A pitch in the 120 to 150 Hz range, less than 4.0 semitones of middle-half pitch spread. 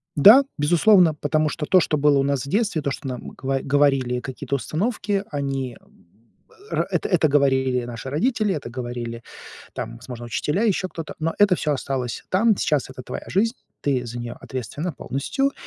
No: medium, 140 Hz; wide, 5.4 semitones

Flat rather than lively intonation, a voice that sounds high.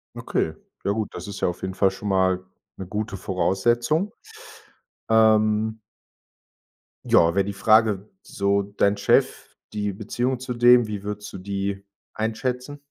No: narrow, 2.3 semitones; low, 105 Hz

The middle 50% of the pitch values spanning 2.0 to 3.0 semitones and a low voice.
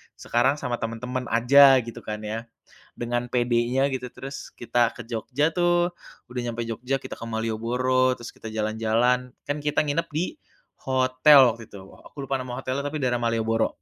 Yes: narrow, 2.5 semitones; low, 125 Hz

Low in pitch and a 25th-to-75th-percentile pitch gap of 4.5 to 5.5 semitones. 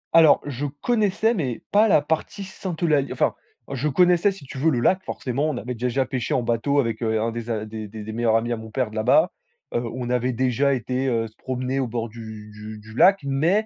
Yes: low, 125 Hz; average, 5.0 semitones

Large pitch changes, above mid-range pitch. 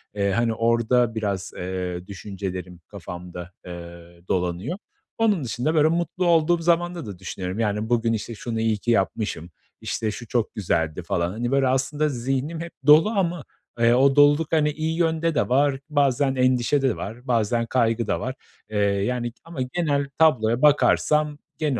No: wide, 6.7 semitones; low, 120 Hz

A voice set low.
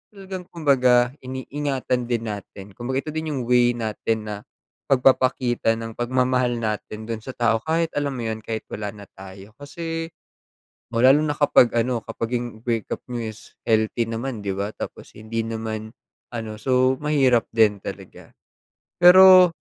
Yes: low, 120 Hz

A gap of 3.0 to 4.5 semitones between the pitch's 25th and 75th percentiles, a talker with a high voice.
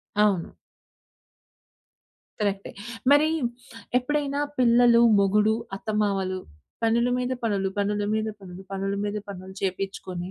Yes: average, 3.3 semitones; high, 205 Hz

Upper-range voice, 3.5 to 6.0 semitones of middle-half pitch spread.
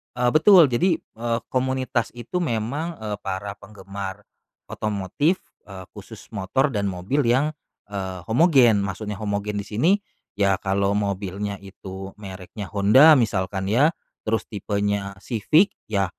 No: low, 105 Hz; average, 4.1 semitones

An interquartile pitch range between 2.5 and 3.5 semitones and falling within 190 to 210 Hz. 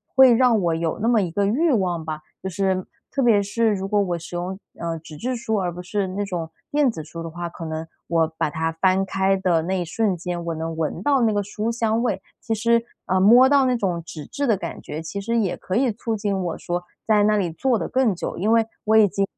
No: average, 4.8 semitones; high, 195 Hz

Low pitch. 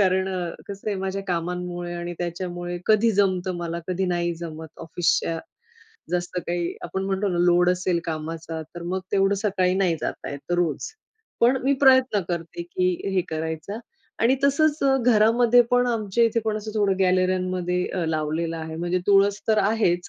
No: medium, 185 Hz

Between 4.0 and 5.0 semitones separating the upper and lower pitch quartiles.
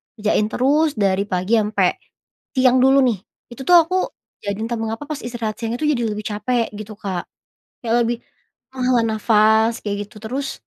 No: average, 3.1 semitones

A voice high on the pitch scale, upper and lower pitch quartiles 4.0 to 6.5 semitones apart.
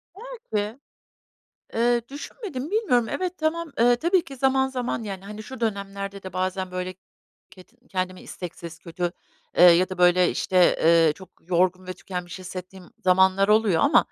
Yes: high, 195 Hz; wide, 5.5 semitones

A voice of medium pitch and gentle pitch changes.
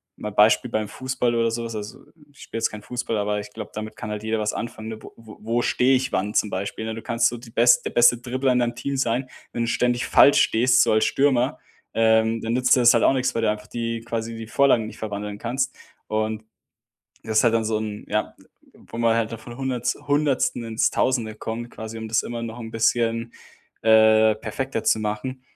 No: low, 115 Hz; narrow, 1.9 semitones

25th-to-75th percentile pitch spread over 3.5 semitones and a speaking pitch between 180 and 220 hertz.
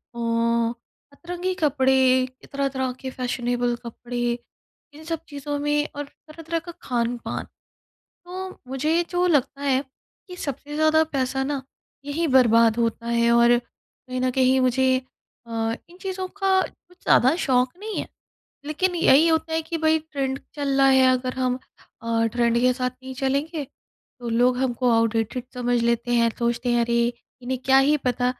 No: average, 3.9 semitones; very high, 260 Hz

